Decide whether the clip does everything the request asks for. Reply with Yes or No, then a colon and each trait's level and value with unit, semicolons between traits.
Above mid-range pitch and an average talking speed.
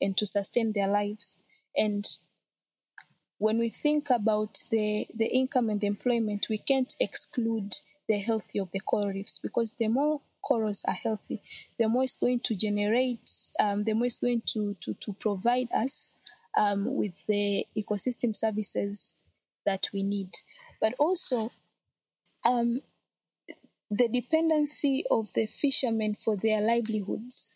Yes: high, 220 Hz; average, 145 wpm